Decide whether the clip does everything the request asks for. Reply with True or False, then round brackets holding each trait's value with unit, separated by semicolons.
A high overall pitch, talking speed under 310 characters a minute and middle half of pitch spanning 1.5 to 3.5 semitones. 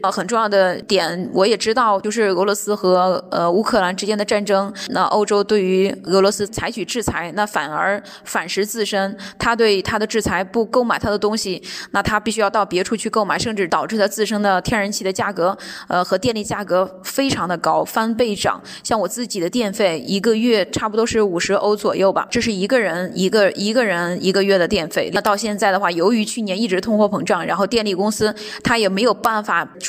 False (205 Hz; 320 characters per minute; 2.4 semitones)